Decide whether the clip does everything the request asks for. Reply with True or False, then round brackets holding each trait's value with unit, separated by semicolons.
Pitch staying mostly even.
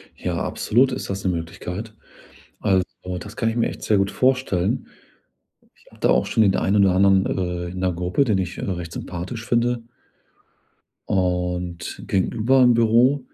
False (4.5 semitones)